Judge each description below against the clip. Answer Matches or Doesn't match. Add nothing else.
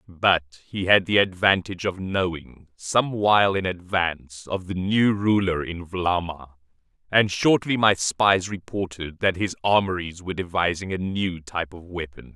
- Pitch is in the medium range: Doesn't match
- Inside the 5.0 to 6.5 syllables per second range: Doesn't match